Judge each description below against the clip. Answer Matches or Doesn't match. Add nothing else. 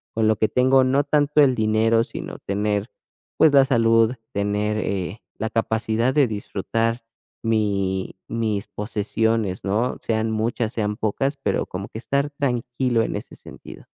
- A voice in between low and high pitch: Doesn't match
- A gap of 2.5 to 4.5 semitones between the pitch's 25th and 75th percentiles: Matches